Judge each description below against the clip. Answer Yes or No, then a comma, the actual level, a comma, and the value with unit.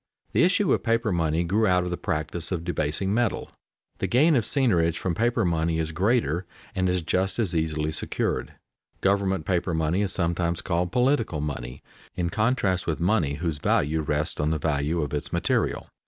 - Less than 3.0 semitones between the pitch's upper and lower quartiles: No, average, 3.8 semitones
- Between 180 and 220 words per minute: Yes, average, 185 wpm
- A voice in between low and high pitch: No, very low, 85 Hz